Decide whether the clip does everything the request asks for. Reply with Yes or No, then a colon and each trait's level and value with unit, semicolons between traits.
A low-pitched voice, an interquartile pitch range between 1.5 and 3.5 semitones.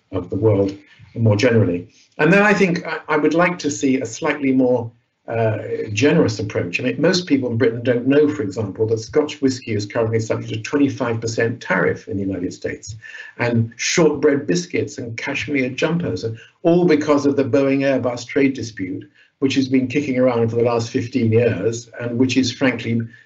No: low, 125 Hz; average, 4.0 semitones